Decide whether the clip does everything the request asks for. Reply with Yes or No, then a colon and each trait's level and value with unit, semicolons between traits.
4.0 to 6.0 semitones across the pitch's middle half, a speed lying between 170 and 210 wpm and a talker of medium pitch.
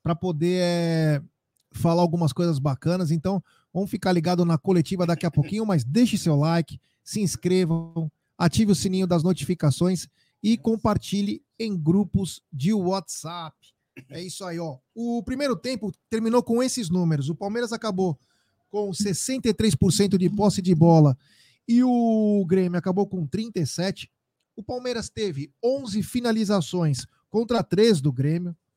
No: average, 4.3 semitones; average, 140 wpm; medium, 180 Hz